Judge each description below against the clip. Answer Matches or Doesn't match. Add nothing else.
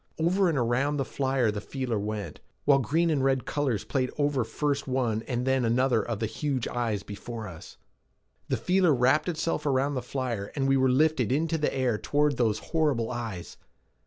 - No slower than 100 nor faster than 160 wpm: Doesn't match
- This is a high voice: Doesn't match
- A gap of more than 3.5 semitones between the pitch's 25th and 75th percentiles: Matches